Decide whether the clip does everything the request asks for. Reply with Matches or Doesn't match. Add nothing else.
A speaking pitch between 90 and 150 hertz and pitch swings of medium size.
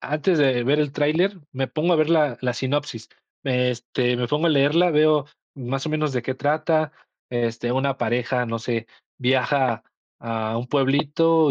Matches